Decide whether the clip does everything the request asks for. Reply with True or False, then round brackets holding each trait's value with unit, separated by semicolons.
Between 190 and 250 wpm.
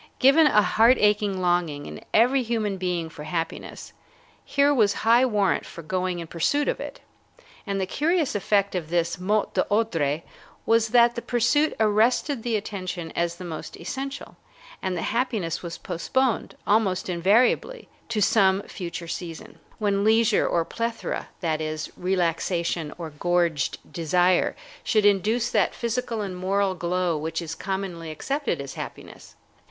False (150 wpm)